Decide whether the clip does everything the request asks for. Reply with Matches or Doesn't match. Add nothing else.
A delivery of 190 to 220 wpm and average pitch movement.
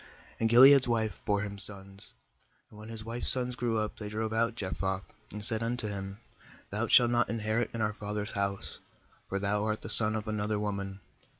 Doesn't match